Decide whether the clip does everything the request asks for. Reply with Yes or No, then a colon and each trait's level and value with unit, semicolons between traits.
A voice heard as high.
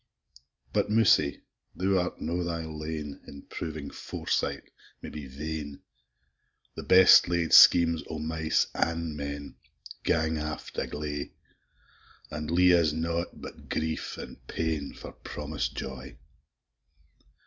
No: very low, 80 Hz